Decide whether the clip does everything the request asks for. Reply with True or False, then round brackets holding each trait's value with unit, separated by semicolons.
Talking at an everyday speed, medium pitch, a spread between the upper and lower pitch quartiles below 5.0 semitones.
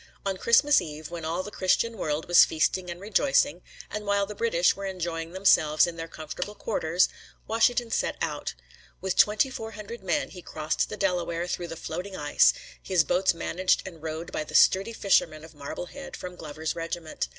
True (185 wpm; 180 Hz; 3.8 semitones)